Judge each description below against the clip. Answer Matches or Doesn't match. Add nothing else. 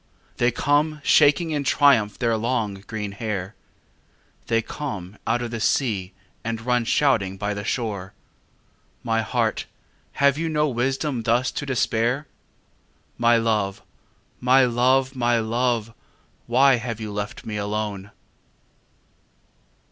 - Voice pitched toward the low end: Matches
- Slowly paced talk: Matches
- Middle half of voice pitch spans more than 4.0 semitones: Doesn't match